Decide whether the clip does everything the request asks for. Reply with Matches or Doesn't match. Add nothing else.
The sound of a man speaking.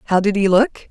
Doesn't match